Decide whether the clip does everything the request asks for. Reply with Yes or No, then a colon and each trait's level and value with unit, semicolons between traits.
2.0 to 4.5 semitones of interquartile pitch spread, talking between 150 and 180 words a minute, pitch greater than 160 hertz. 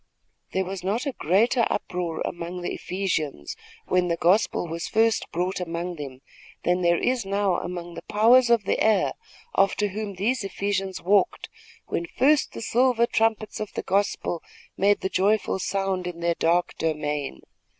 Yes: average, 3.6 semitones; average, 160 wpm; high, 190 Hz